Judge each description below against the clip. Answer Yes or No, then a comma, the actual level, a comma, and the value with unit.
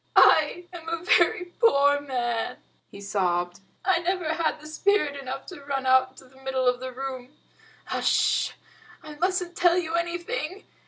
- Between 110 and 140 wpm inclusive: No, average, 155 wpm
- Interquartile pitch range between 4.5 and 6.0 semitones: Yes, average, 5.0 semitones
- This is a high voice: Yes, very high, 285 Hz